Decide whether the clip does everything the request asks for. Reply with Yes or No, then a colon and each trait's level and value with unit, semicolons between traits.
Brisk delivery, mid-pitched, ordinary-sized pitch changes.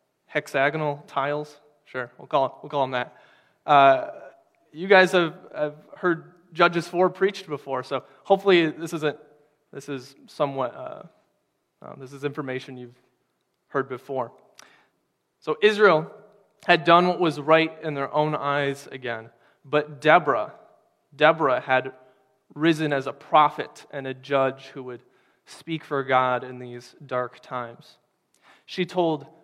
No: average, 140 wpm; medium, 145 Hz; average, 3.6 semitones